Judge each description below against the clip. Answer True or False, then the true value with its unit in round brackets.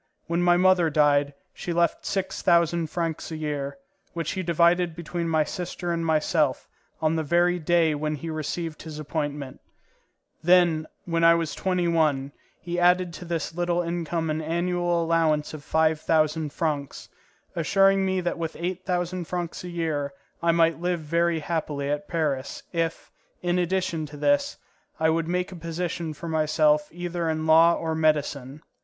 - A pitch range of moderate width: False (2.1 semitones)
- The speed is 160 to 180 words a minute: True (165 wpm)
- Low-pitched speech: False (165 Hz)